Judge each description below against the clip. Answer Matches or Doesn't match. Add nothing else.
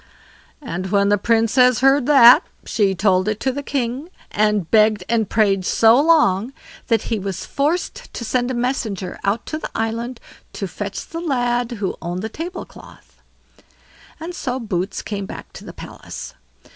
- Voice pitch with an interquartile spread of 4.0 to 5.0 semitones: Matches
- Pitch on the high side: Matches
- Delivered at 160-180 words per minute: Matches